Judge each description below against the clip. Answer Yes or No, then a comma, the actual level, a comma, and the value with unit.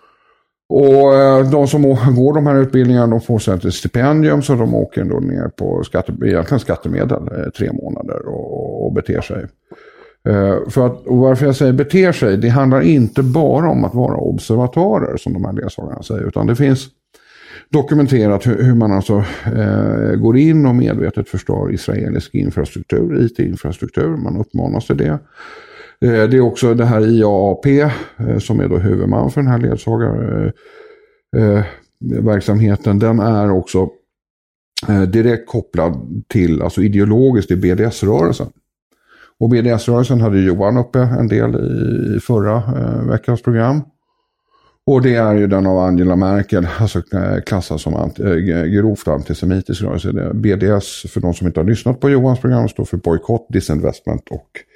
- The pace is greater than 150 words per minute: No, average, 145 wpm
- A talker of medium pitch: No, low, 115 Hz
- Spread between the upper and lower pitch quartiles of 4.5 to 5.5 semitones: Yes, average, 5.0 semitones